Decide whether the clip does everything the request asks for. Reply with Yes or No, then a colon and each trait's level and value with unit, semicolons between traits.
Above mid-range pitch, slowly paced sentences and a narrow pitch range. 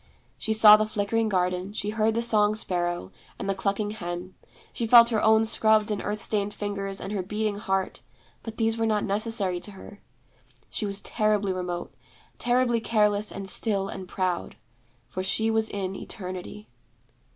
No: high, 210 Hz; average, 170 wpm; narrow, 2.3 semitones